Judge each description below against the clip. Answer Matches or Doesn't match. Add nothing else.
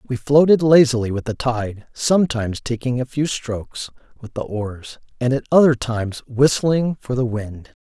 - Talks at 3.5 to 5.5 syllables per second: Matches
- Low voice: Matches